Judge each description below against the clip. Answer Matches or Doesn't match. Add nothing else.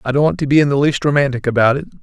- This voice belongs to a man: Matches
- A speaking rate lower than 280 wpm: Doesn't match